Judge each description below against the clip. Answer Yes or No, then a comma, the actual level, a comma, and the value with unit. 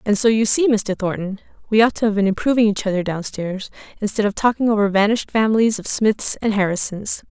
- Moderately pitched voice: No, high, 210 Hz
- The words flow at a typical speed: No, fast, 215 wpm